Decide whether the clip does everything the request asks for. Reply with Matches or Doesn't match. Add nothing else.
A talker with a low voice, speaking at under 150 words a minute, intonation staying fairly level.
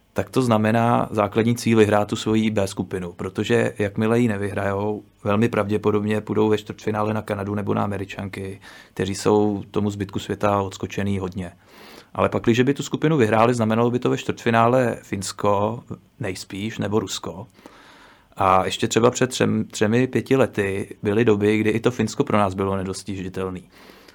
Doesn't match